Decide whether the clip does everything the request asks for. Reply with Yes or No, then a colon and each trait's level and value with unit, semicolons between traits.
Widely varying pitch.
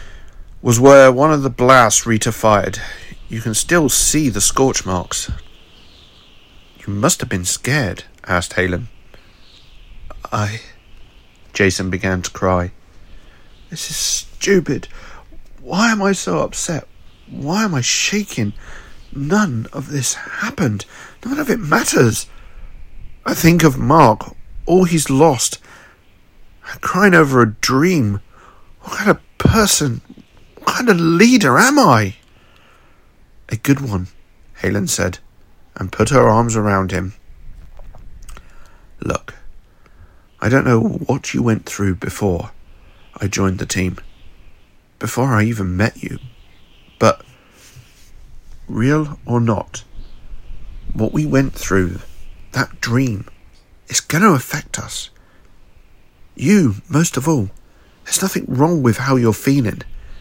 Yes: wide, 6.9 semitones